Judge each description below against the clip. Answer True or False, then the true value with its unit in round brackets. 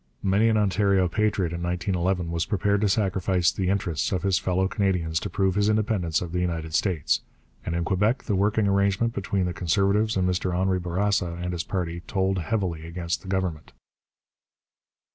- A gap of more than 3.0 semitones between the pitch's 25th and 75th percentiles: False (2.5 semitones)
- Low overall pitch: True (95 Hz)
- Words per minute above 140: True (180 wpm)